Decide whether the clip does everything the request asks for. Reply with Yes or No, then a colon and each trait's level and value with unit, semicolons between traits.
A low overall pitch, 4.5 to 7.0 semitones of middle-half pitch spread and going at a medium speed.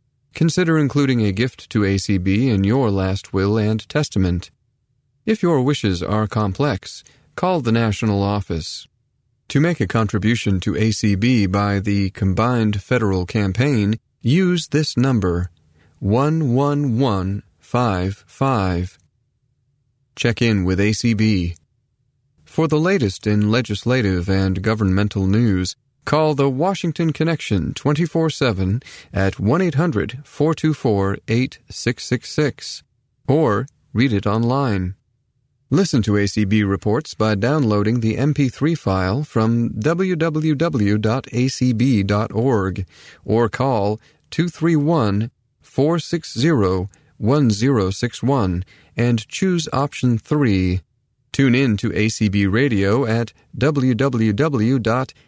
No: low, 115 Hz; average, 5.2 semitones; slow, 100 wpm